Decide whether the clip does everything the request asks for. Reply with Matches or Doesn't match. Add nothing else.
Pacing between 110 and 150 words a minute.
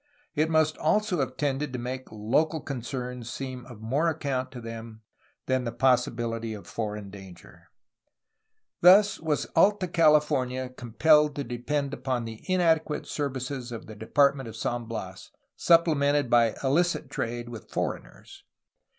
Matches